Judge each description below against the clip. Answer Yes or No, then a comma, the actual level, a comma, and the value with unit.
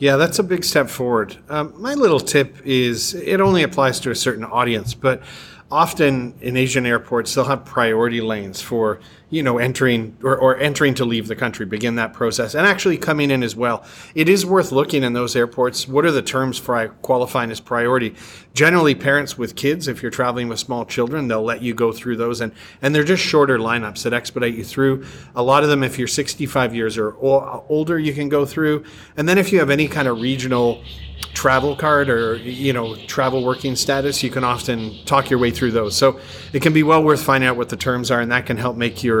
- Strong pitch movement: No, average, 3.3 semitones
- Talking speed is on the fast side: Yes, fast, 220 wpm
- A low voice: Yes, low, 130 Hz